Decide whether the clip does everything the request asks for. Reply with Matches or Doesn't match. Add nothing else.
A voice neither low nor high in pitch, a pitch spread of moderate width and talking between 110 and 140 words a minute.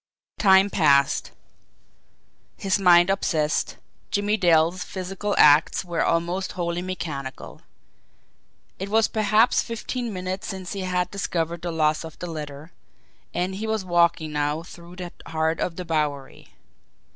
Matches